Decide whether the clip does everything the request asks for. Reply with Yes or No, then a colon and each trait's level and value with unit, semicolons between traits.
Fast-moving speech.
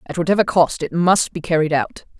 Yes: fast, 220 wpm